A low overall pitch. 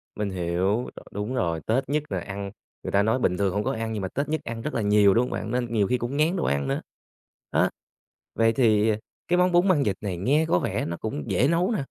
Yes: low, 115 Hz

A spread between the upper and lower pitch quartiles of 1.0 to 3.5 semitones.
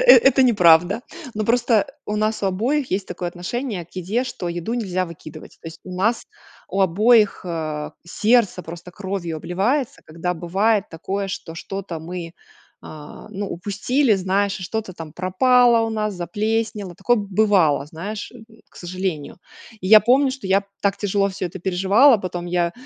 No: average, 3.9 semitones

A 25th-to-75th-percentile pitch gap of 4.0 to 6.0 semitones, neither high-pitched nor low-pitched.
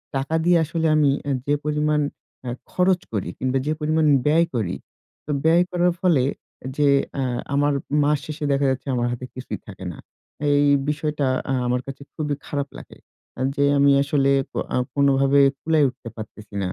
No: narrow, 2.4 semitones; medium, 145 Hz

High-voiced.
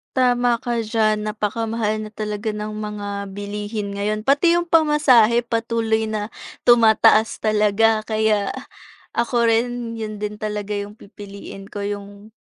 Yes: high, 215 Hz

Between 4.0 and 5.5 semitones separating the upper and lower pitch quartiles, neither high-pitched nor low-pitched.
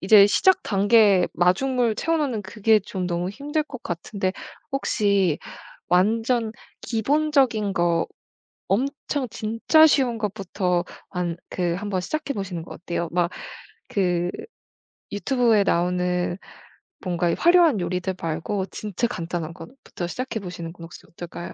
No: average, 5.1 semitones; high, 200 Hz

